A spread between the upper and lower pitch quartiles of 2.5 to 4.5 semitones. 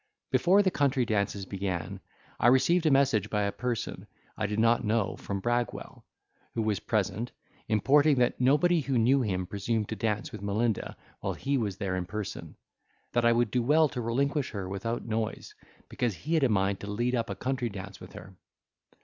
Yes: average, 4.1 semitones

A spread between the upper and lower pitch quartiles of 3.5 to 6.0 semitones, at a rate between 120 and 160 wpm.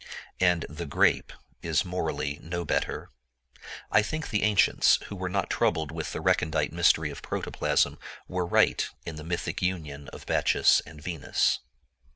No: average, 3.0 semitones; average, 155 wpm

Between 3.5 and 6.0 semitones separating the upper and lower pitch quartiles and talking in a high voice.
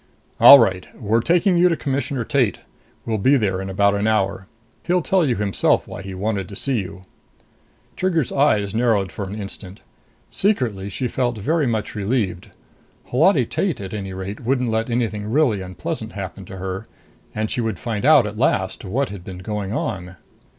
No: average, 4.7 semitones; low, 110 Hz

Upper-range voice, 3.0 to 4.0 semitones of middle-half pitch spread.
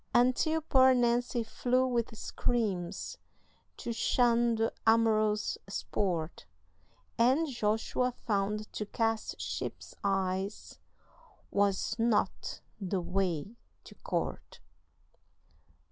Yes: high, 225 Hz; average, 3.3 semitones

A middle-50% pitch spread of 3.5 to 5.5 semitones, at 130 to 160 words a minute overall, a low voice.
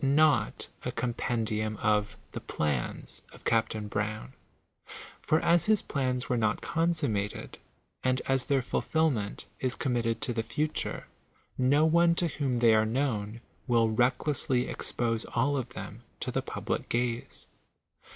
Yes: average, 4.3 semitones; average, 145 wpm; low, 125 Hz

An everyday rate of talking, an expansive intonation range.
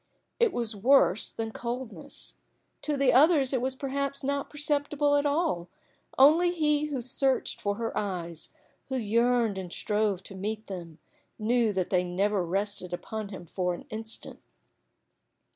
Yes: average, 150 wpm; wide, 6.0 semitones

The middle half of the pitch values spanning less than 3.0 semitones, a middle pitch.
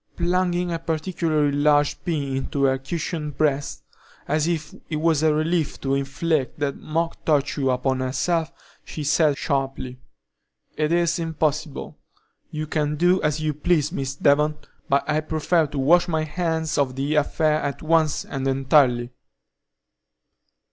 Yes: narrow, 2.6 semitones; medium, 150 Hz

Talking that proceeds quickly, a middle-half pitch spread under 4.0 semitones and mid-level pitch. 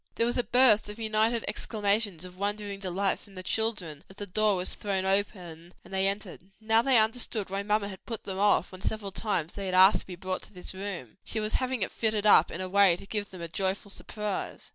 No: fast, 235 wpm; narrow, 2.4 semitones; high, 200 Hz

